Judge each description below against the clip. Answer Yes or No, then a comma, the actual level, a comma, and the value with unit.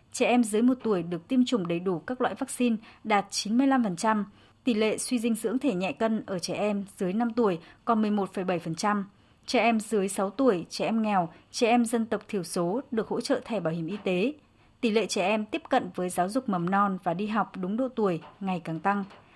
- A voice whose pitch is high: Yes, high, 210 Hz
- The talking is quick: No, average, 225 wpm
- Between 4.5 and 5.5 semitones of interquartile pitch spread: No, average, 4.1 semitones